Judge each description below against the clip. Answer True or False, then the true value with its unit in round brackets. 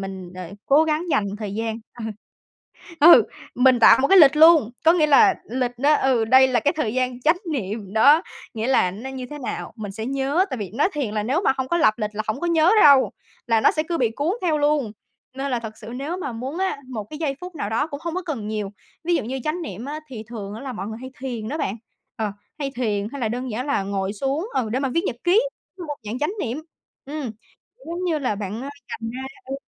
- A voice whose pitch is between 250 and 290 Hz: True (260 Hz)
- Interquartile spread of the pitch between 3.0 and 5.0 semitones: False (5.4 semitones)